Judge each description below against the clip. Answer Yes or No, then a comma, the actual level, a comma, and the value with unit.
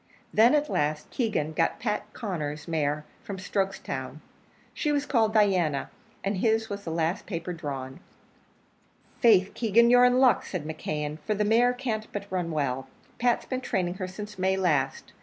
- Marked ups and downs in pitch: Yes, wide, 6.2 semitones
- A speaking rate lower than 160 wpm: No, average, 165 wpm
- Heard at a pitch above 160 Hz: Yes, high, 190 Hz